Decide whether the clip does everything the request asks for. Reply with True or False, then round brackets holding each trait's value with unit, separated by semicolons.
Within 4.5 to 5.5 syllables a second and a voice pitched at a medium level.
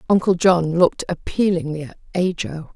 True (5.3 syllables/s; 170 Hz)